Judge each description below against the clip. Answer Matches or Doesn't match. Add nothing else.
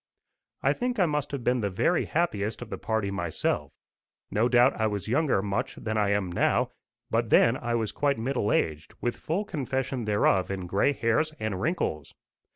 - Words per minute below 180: Doesn't match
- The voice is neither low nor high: Doesn't match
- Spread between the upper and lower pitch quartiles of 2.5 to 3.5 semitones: Doesn't match